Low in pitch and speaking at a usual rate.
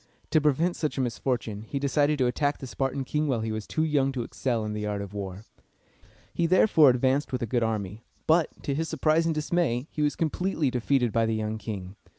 No: low, 130 Hz; fast, 220 wpm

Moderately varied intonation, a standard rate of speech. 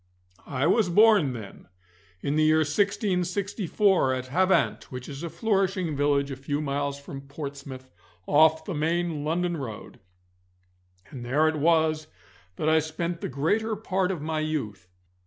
Yes: average, 4.1 semitones; average, 150 wpm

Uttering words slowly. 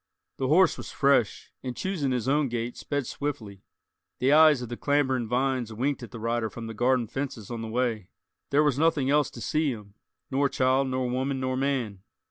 No: average, 200 wpm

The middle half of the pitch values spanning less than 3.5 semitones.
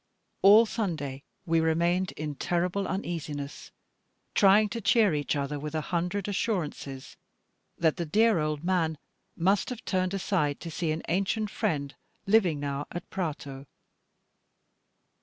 No: average, 4.7 semitones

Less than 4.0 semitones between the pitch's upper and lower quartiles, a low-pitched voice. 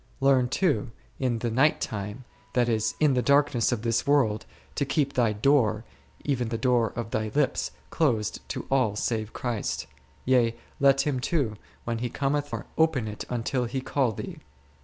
Yes: average, 3.5 semitones; low, 125 Hz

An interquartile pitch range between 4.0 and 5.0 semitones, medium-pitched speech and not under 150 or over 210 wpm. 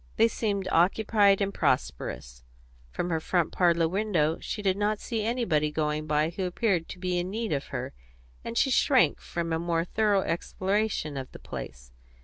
Yes: average, 4.7 semitones; medium, 180 Hz; average, 175 wpm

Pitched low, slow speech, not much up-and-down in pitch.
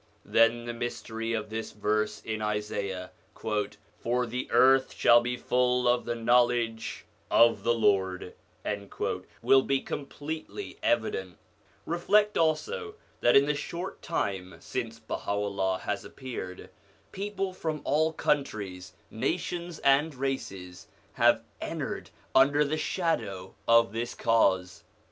No: low, 120 Hz; slow, 120 wpm; average, 5.3 semitones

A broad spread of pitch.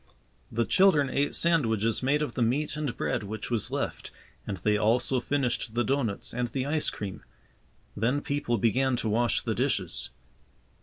No: average, 4.1 semitones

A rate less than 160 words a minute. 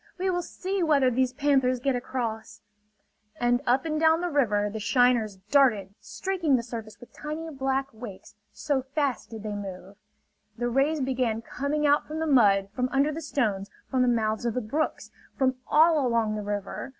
No: average, 185 wpm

